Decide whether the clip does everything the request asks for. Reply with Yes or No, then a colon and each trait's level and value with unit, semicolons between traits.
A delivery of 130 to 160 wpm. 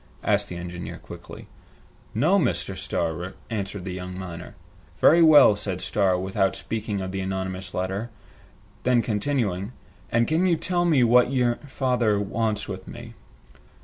Yes: average, 145 wpm